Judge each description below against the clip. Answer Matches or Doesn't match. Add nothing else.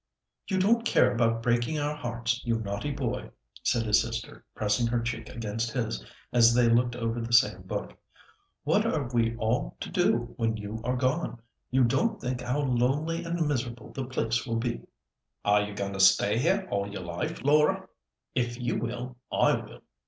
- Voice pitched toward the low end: Matches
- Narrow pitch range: Matches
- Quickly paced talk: Doesn't match